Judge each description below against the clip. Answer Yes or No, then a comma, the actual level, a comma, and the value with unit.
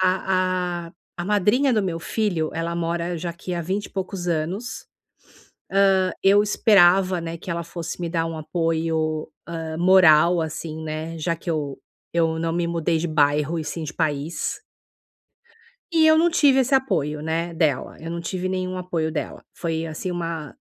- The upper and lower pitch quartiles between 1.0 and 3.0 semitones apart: Yes, narrow, 2.4 semitones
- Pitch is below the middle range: No, medium, 170 Hz